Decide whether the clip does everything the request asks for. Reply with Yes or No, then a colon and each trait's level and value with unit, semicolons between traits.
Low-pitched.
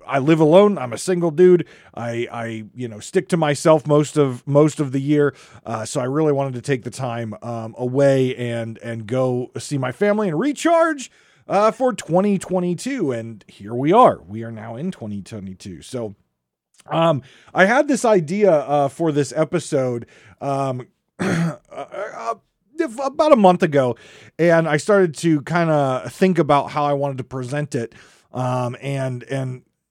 No: medium, 145 Hz